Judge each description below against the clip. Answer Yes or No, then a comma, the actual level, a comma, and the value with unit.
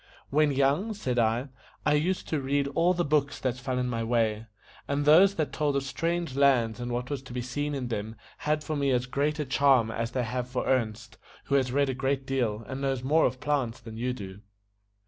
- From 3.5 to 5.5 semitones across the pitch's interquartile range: No, average, 3.1 semitones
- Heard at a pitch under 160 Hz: Yes, low, 135 Hz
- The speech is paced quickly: Yes, fast, 225 wpm